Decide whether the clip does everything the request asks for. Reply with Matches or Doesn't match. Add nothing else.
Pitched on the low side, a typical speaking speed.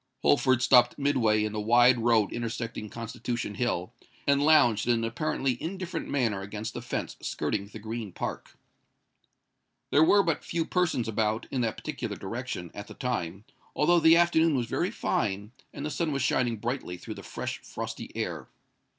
Matches